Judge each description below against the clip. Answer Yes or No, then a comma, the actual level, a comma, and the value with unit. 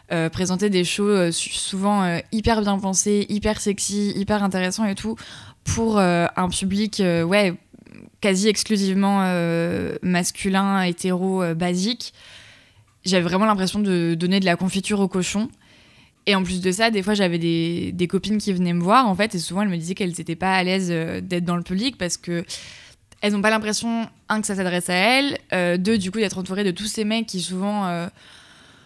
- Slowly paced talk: No, average, 200 wpm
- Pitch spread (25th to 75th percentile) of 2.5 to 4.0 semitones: Yes, average, 2.8 semitones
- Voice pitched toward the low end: No, high, 190 Hz